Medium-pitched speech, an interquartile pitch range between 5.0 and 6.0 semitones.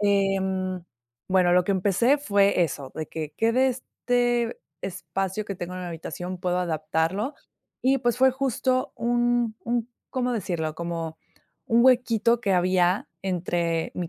No: high, 195 Hz; wide, 5.4 semitones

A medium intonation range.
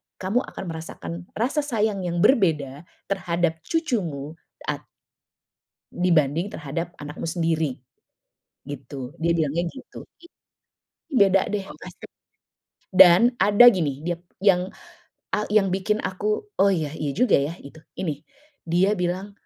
Yes: average, 4.3 semitones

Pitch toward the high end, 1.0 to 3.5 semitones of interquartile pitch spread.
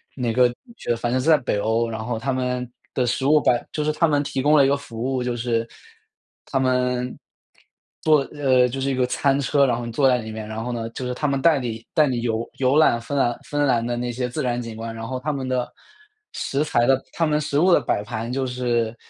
No: low, 125 Hz; average, 2.7 semitones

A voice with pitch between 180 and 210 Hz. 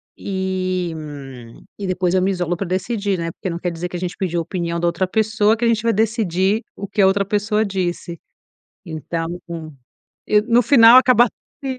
Yes: high, 190 Hz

